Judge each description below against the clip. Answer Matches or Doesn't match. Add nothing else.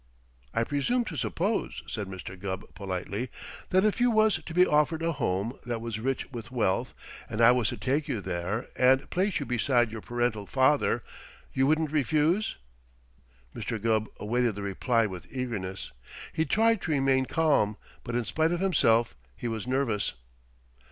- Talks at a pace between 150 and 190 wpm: Matches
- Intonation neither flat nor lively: Doesn't match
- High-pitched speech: Doesn't match